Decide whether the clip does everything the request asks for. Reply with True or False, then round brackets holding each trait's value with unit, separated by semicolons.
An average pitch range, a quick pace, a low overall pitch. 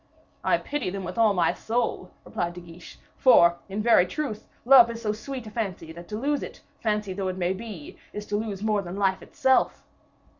False (4.0 semitones; 210 wpm; 210 Hz)